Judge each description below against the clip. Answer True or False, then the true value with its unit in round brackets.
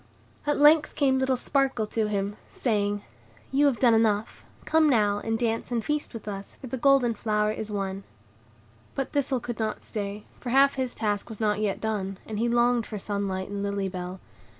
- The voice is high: True (220 Hz)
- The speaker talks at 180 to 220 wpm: True (195 wpm)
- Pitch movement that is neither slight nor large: True (4.0 semitones)